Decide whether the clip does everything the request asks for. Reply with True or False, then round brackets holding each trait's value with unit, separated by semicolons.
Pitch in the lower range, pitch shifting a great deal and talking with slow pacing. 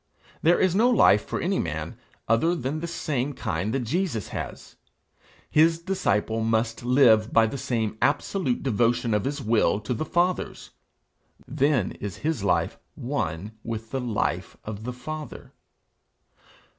False (125 Hz; 5.7 semitones; 145 wpm)